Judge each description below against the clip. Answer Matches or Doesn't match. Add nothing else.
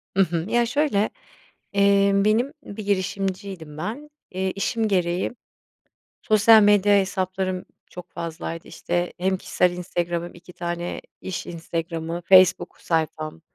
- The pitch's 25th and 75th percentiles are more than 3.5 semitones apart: Doesn't match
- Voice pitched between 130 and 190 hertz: Matches